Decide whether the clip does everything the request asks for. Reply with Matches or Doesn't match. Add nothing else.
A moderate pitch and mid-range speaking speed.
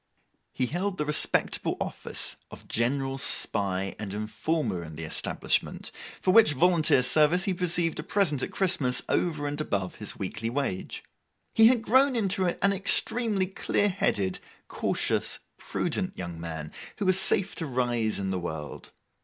Matches